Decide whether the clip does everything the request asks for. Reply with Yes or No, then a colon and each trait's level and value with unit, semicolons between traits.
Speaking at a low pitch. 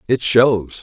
Yes: low, 120 Hz